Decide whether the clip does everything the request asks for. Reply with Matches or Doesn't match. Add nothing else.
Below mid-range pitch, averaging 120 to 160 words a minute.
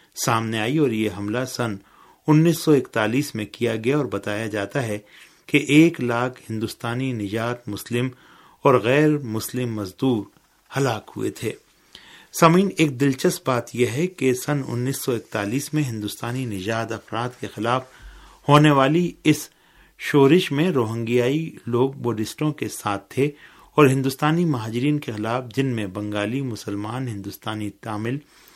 Matches